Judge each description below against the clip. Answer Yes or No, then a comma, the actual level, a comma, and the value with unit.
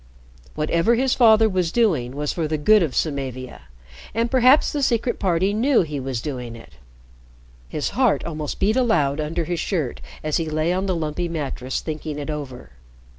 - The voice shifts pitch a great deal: Yes, wide, 6.7 semitones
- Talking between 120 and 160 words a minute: No, average, 175 wpm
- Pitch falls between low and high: Yes, medium, 165 Hz